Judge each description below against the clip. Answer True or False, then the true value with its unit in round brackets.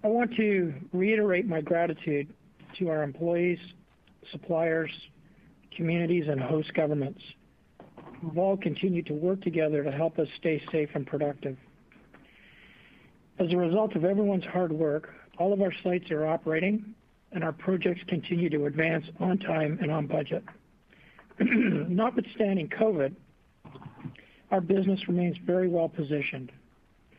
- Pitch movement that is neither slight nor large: True (3.4 semitones)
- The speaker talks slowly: True (130 wpm)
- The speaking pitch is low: False (170 Hz)